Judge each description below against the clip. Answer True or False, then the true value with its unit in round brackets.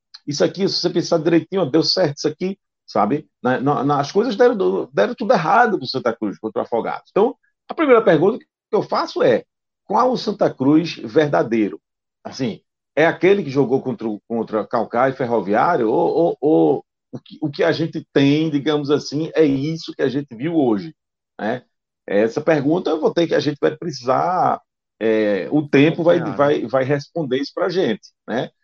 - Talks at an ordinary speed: False (190 wpm)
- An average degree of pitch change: True (3.8 semitones)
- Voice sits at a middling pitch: True (155 Hz)